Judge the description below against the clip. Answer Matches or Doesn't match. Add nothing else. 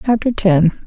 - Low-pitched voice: Doesn't match